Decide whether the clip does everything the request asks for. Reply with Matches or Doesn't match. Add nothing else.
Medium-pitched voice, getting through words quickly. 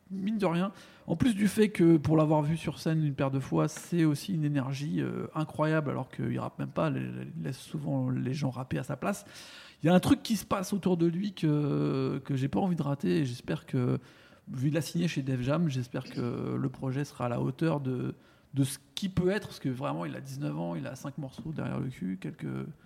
Matches